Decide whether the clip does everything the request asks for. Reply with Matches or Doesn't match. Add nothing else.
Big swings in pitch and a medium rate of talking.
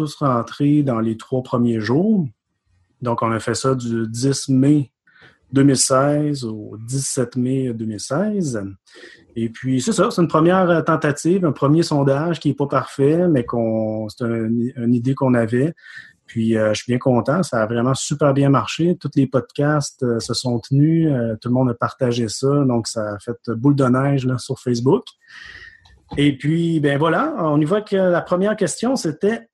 Doesn't match